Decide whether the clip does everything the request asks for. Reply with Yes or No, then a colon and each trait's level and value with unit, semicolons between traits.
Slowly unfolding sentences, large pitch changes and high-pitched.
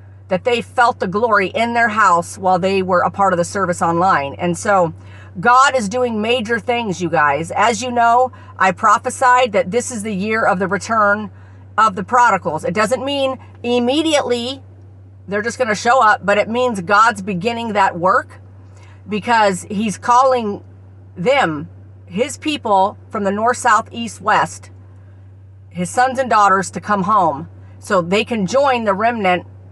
No: average, 170 wpm; wide, 5.9 semitones; high, 205 Hz